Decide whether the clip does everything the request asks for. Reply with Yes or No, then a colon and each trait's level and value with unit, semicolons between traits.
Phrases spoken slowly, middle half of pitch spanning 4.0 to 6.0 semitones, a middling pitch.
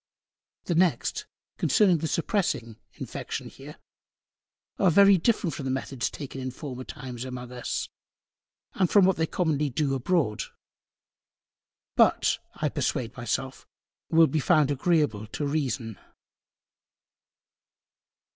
Yes: slow, 120 wpm; average, 4.9 semitones; medium, 145 Hz